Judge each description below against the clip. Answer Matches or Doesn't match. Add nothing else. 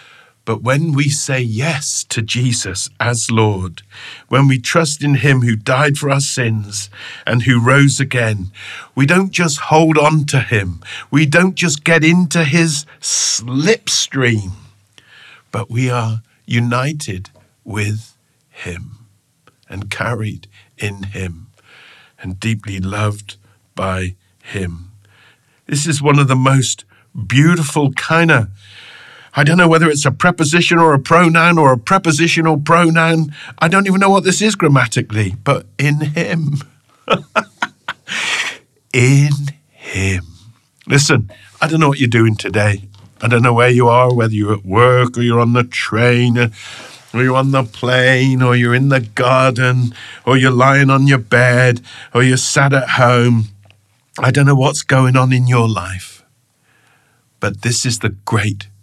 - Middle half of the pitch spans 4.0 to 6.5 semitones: Matches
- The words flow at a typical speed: Matches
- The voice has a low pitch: Matches